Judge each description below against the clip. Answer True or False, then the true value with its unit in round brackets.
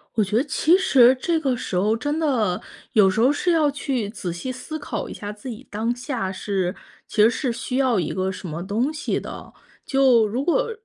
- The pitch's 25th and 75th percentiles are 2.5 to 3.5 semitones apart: False (5.3 semitones)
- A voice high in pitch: True (240 Hz)